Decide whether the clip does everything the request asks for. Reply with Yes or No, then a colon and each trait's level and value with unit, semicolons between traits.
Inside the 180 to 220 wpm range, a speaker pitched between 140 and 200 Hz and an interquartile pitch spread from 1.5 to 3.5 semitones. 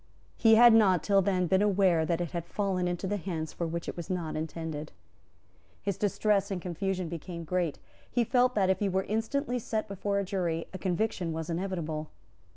Yes: average, 190 wpm; medium, 185 Hz; average, 3.1 semitones